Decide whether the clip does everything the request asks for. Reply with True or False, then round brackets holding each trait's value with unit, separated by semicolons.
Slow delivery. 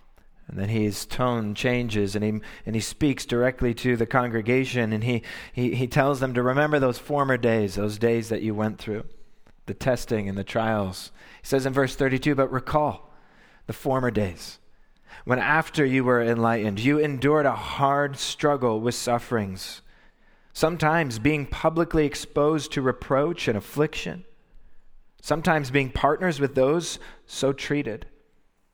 False (150 wpm)